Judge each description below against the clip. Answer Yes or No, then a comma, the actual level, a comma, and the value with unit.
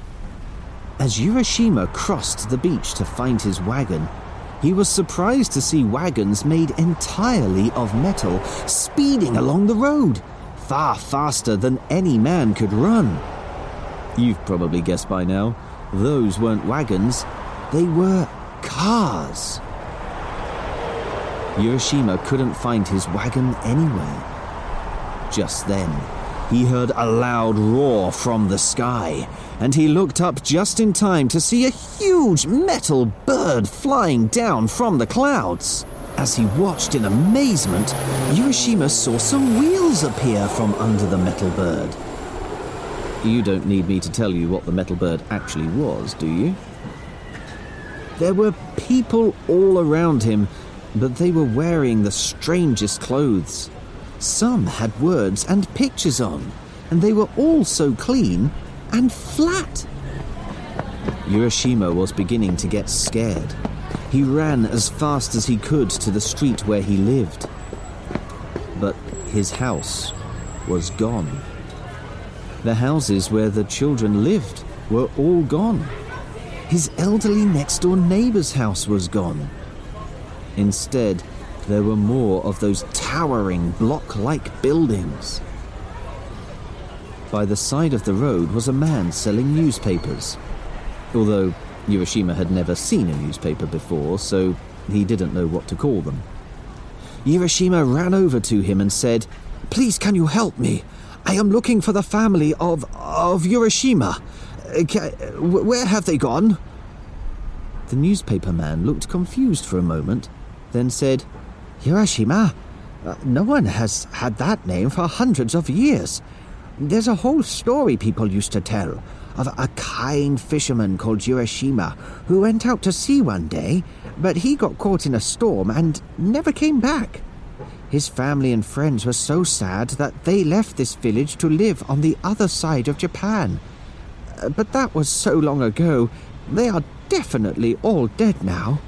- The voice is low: Yes, low, 120 Hz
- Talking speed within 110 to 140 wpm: Yes, slow, 135 wpm